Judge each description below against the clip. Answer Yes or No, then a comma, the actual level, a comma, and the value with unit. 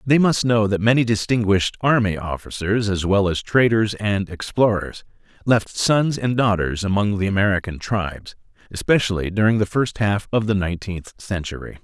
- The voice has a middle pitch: No, low, 105 Hz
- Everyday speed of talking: Yes, average, 155 wpm